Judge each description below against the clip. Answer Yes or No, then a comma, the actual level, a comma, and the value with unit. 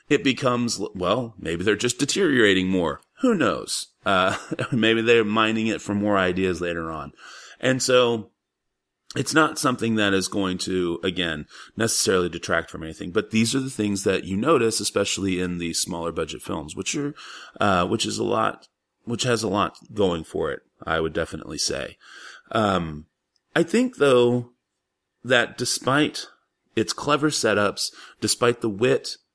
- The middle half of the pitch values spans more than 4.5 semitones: Yes, wide, 5.4 semitones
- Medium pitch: No, low, 105 Hz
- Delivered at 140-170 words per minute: Yes, average, 160 wpm